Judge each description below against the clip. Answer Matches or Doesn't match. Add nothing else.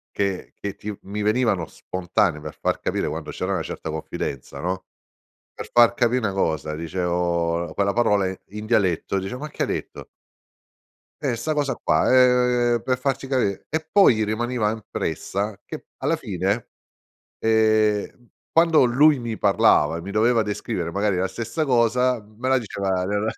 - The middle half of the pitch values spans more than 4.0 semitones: Matches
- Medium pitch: Doesn't match